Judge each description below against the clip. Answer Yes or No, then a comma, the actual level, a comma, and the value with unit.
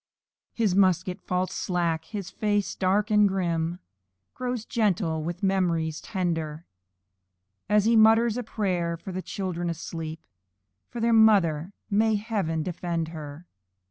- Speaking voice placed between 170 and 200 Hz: Yes, medium, 185 Hz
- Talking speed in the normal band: No, slow, 130 wpm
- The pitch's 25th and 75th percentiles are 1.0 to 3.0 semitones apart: No, average, 4.0 semitones